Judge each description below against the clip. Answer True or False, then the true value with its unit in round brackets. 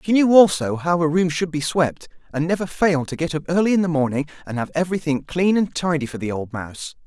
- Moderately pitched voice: True (160 Hz)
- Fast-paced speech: True (245 wpm)